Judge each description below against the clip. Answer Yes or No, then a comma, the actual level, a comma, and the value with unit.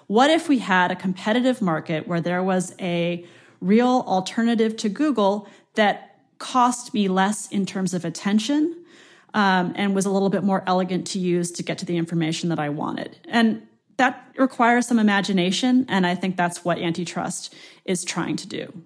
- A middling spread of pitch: Yes, average, 4.8 semitones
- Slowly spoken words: No, average, 180 wpm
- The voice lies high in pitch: Yes, high, 195 Hz